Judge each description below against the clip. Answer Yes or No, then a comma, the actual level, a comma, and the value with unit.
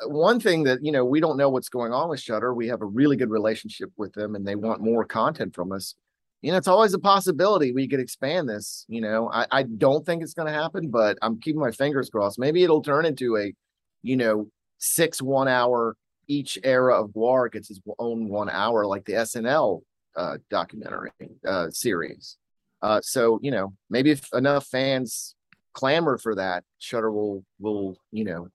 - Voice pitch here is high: No, low, 125 Hz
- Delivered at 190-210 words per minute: Yes, average, 200 wpm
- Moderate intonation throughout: Yes, average, 4.7 semitones